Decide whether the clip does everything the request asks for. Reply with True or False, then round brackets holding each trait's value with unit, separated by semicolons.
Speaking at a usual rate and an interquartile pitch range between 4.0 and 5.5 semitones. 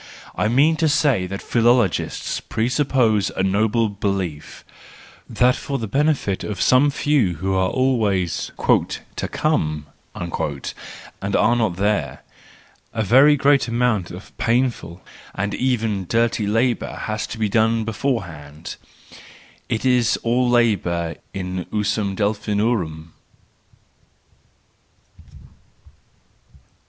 False (110 wpm; 4.5 semitones)